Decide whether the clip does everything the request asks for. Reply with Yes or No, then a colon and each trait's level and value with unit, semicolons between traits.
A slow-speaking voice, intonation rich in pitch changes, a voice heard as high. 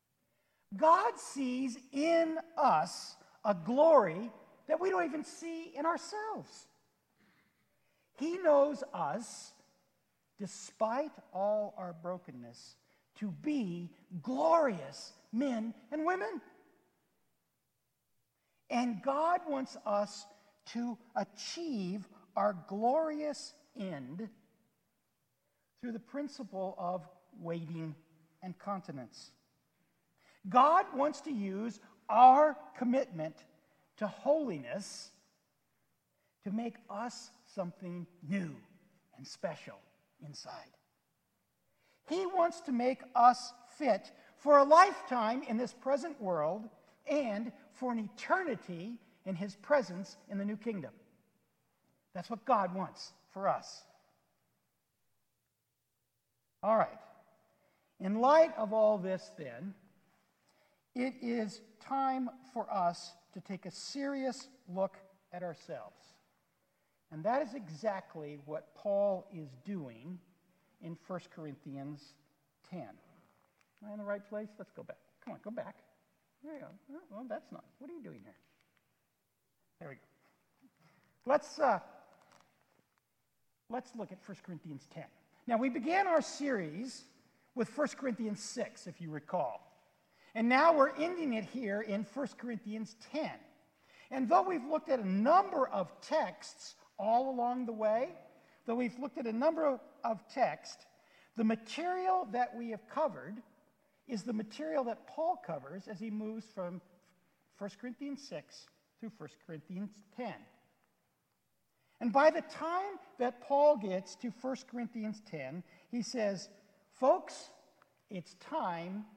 Yes: slow, 120 wpm; wide, 6.6 semitones; high, 225 Hz